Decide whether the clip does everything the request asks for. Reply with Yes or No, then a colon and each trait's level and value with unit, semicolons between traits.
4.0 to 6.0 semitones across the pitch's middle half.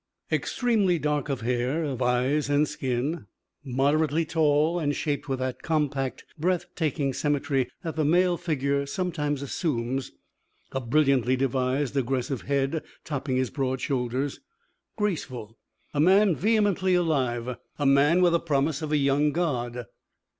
No: average, 3.5 semitones